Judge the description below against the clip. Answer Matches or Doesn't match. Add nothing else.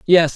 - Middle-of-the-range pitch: Matches